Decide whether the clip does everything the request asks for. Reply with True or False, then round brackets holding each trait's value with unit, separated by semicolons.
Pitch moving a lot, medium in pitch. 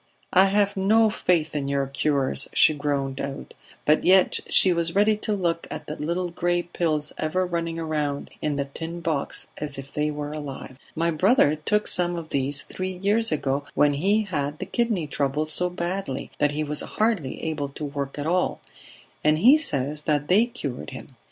False (4.1 semitones; 155 Hz)